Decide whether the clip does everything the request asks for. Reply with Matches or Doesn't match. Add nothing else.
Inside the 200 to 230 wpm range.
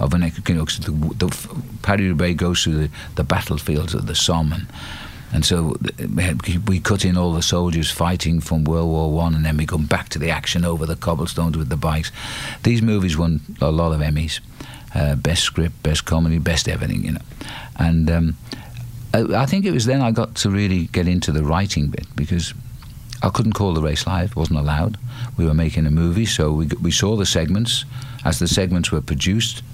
Matches